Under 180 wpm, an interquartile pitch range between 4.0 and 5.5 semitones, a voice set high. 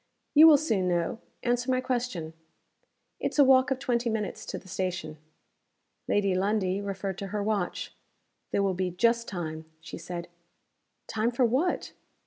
Yes: average, 155 wpm; average, 5.0 semitones; high, 205 Hz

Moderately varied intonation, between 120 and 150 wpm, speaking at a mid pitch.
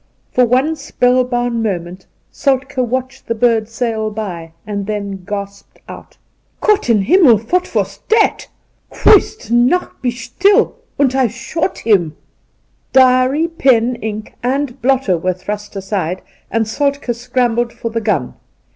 No: average, 4.0 semitones; average, 140 wpm; high, 240 Hz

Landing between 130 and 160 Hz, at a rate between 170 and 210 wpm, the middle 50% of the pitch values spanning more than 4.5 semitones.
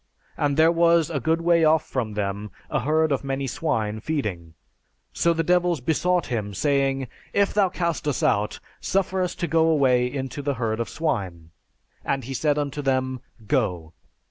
Yes: medium, 140 Hz; average, 175 wpm; wide, 5.6 semitones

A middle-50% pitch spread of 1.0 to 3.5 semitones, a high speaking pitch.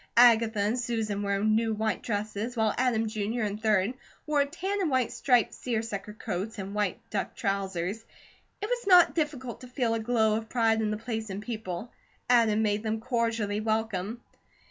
Yes: narrow, 2.5 semitones; high, 220 Hz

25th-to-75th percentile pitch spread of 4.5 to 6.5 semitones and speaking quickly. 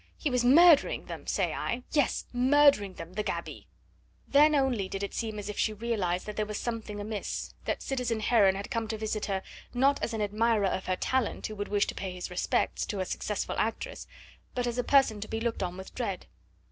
No: average, 3.5 semitones; fast, 220 wpm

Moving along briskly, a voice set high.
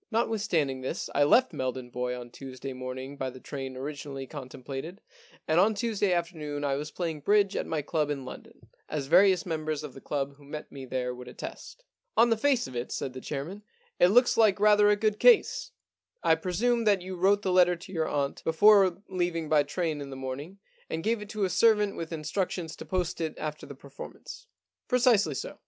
No: fast, 215 wpm; medium, 160 Hz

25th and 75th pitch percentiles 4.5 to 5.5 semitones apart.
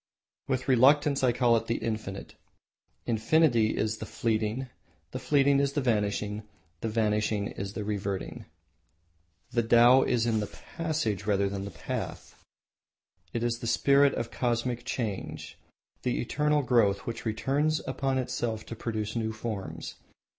No: average, 3.4 semitones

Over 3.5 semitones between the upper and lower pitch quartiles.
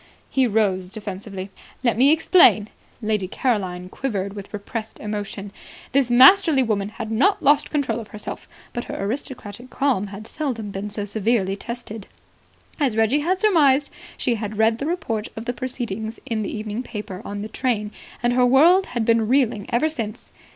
Yes: average, 4.0 semitones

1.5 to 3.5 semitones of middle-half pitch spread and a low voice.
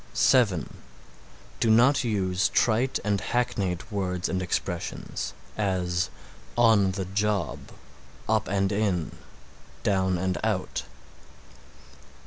Yes: average, 2.9 semitones; low, 100 Hz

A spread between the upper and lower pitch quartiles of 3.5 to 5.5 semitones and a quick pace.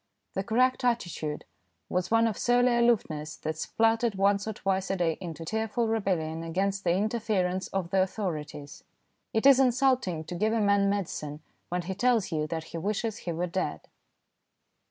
No: average, 4.8 semitones; average, 170 wpm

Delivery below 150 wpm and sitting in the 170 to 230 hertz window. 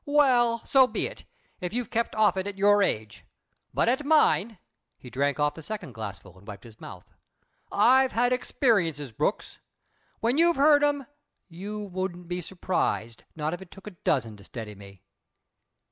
No: average, 175 wpm; high, 190 Hz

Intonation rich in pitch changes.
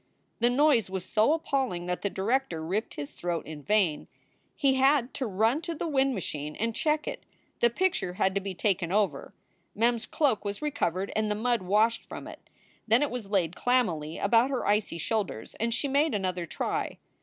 Yes: wide, 5.8 semitones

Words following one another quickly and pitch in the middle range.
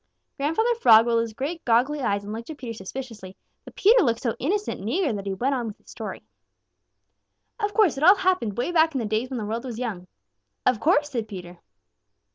No: fast, 220 wpm; high, 245 Hz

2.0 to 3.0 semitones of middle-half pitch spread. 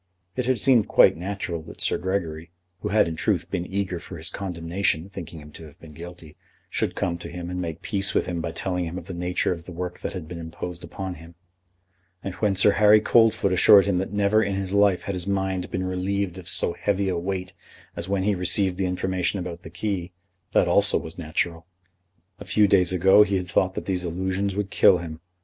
Yes: narrow, 2.4 semitones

